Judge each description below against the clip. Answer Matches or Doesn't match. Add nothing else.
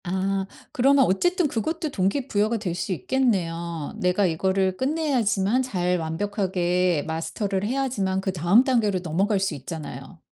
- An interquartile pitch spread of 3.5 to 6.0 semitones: Matches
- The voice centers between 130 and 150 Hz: Doesn't match